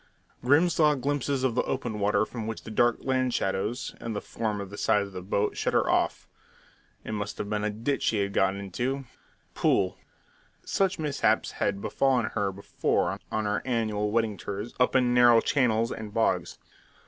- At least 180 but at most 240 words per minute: Yes, average, 185 wpm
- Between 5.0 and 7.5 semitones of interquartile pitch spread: No, average, 3.7 semitones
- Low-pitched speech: Yes, low, 110 Hz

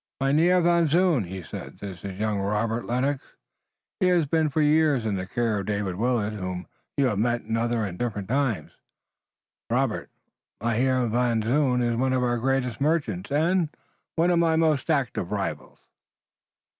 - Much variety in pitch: Yes, wide, 5.7 semitones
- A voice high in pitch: No, low, 120 Hz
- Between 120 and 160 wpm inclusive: No, average, 170 wpm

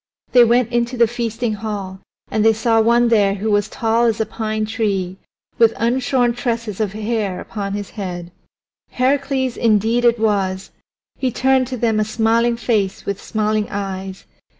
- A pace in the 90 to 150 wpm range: No, average, 165 wpm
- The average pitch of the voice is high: Yes, high, 220 Hz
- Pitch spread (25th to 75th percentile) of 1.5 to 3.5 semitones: Yes, narrow, 2.5 semitones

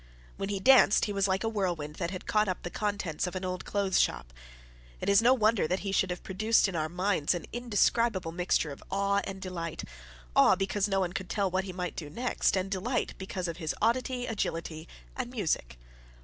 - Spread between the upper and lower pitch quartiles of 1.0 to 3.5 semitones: Yes, average, 2.8 semitones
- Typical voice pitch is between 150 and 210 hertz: Yes, high, 190 Hz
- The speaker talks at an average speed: No, fast, 215 wpm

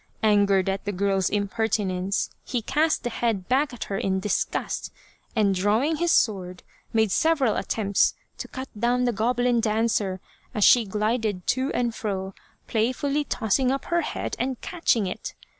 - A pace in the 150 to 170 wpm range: Yes, average, 160 wpm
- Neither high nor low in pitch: No, high, 220 Hz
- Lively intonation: No, average, 4.0 semitones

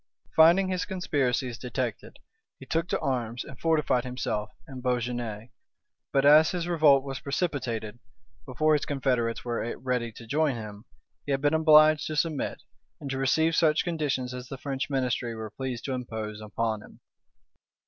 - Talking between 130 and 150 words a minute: No, average, 160 wpm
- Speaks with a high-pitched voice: No, low, 130 Hz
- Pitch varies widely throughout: No, average, 4.2 semitones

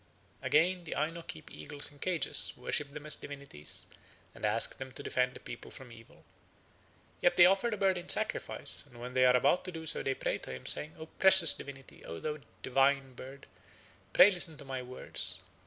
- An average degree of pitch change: Yes, average, 4.5 semitones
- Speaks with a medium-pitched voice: Yes, medium, 145 Hz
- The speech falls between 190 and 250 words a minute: Yes, average, 200 wpm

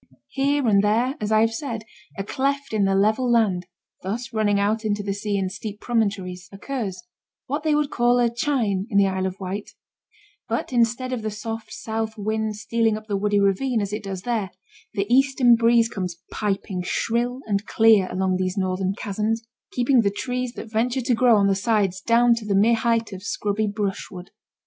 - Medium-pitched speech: No, high, 215 Hz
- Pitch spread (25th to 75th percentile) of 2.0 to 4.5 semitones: Yes, average, 3.1 semitones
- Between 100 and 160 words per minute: No, average, 195 wpm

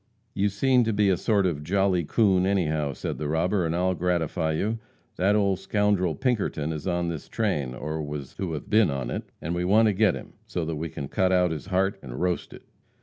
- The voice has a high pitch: No, very low, 90 Hz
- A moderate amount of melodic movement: Yes, average, 4.2 semitones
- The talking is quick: Yes, fast, 225 wpm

